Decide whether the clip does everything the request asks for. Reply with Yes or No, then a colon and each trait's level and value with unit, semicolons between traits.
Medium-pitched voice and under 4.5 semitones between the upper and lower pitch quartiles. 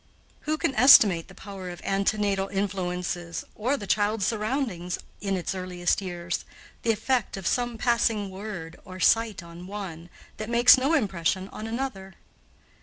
No: high, 195 Hz; average, 3.8 semitones